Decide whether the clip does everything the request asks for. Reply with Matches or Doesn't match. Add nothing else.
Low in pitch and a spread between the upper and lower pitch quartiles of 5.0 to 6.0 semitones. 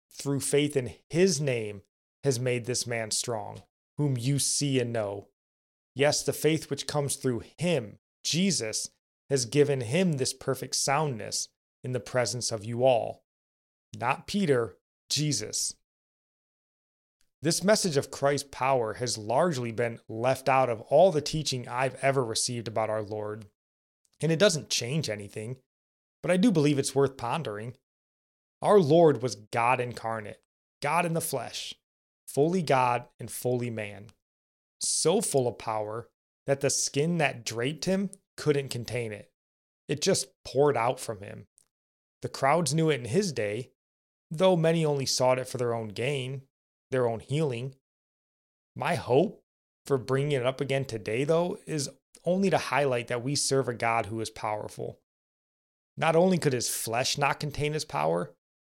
Doesn't match